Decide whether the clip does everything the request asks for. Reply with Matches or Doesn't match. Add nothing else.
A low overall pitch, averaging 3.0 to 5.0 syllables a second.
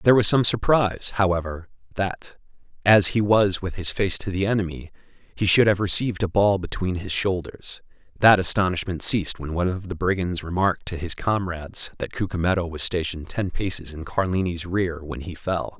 Doesn't match